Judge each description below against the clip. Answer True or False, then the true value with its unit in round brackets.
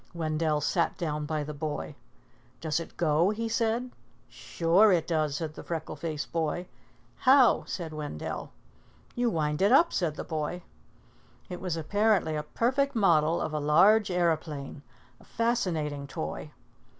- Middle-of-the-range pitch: True (165 Hz)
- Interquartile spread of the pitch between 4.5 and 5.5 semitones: True (5.1 semitones)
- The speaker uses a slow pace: False (150 wpm)